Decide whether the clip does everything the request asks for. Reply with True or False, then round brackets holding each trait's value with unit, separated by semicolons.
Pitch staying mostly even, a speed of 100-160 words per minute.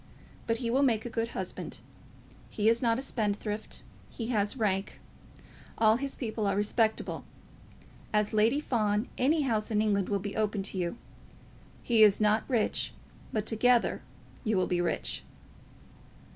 True (2.1 semitones; 155 wpm)